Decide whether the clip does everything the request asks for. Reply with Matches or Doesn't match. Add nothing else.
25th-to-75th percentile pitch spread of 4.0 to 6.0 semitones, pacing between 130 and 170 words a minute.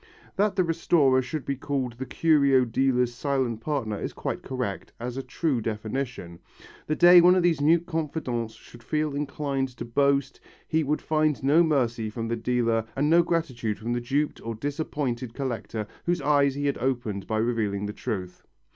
Doesn't match